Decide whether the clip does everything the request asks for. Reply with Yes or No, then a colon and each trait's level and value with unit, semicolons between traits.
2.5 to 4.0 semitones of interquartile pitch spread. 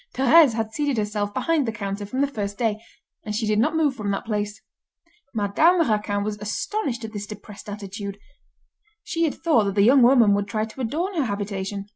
No: average, 4.6 semitones